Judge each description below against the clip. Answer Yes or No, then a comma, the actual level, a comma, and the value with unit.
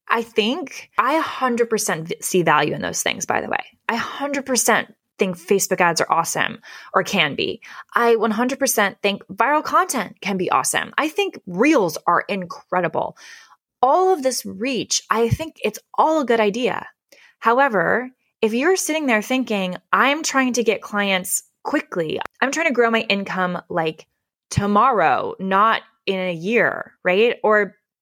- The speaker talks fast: No, average, 155 wpm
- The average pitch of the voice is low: No, high, 230 Hz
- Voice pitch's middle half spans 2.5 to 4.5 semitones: No, average, 5.0 semitones